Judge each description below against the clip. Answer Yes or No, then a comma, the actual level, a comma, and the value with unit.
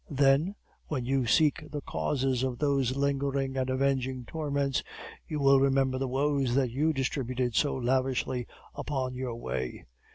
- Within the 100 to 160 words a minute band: Yes, average, 150 wpm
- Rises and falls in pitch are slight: Yes, narrow, 1.6 semitones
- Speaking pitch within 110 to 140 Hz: Yes, low, 135 Hz